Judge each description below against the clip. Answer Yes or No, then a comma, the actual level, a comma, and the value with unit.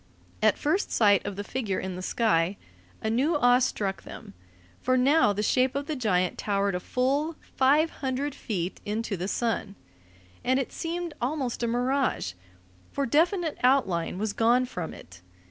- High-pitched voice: Yes, high, 245 Hz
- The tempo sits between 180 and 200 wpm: No, average, 165 wpm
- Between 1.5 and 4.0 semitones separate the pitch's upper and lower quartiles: No, wide, 5.6 semitones